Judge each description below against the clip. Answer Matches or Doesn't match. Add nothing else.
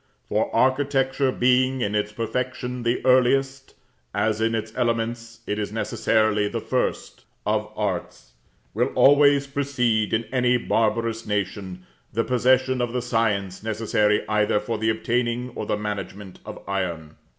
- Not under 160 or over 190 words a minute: Doesn't match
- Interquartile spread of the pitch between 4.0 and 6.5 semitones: Doesn't match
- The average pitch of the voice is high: Doesn't match